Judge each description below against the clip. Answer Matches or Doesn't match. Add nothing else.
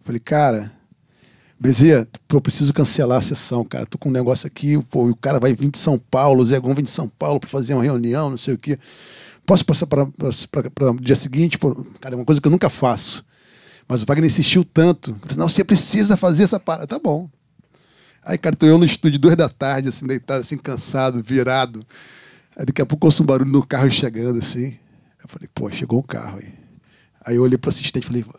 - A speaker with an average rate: Doesn't match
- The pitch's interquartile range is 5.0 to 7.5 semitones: Doesn't match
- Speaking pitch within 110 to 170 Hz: Matches